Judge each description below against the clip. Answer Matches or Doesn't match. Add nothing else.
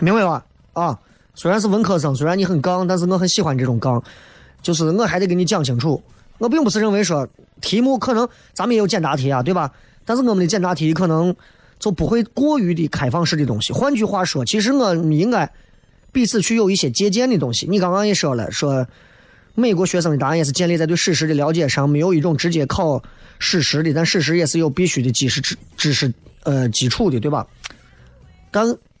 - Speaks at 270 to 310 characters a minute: Doesn't match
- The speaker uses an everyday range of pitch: Doesn't match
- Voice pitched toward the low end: Doesn't match